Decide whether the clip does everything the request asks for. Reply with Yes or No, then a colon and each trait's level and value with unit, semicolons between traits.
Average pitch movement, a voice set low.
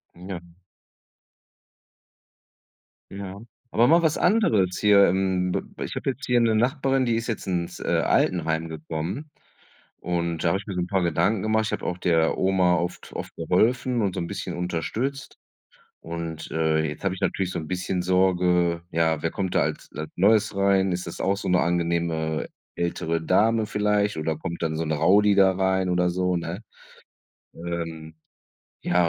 Yes: average, 3.3 semitones; very low, 90 Hz